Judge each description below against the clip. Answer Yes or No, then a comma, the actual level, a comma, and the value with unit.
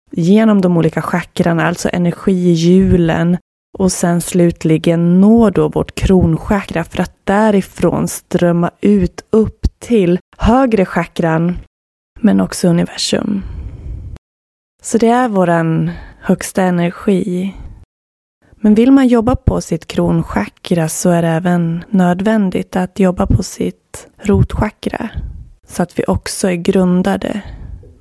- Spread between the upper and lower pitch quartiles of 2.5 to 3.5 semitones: Yes, average, 2.9 semitones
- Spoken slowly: Yes, slow, 115 wpm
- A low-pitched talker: No, medium, 175 Hz